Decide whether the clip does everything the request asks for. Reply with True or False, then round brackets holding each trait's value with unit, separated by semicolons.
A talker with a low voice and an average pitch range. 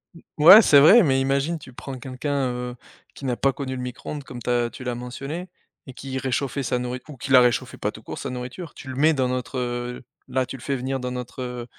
False (130 Hz; 1.9 semitones)